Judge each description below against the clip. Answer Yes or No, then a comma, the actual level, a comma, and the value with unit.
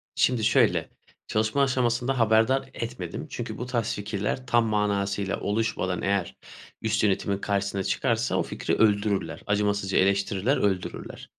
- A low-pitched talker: Yes, low, 105 Hz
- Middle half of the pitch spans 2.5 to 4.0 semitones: Yes, average, 2.9 semitones